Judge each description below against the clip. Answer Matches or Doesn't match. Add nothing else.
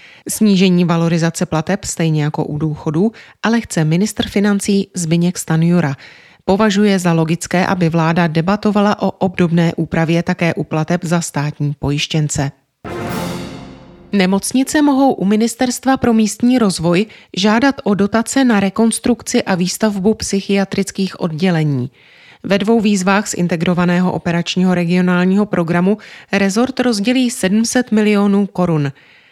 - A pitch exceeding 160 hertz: Matches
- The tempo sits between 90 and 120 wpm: Matches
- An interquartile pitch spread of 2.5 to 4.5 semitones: Matches